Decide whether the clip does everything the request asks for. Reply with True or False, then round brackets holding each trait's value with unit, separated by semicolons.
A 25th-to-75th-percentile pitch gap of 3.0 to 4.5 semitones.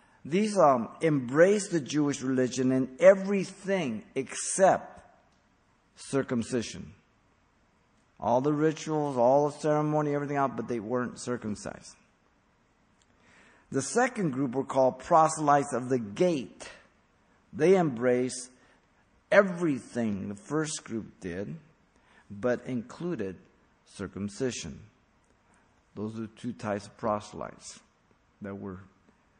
False (5.3 semitones)